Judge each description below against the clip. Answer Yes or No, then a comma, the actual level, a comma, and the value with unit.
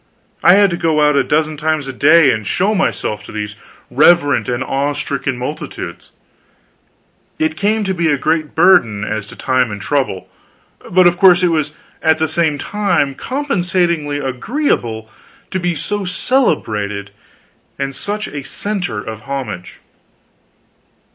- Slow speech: No, average, 150 wpm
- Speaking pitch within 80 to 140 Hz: No, medium, 150 Hz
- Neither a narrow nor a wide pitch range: No, wide, 5.9 semitones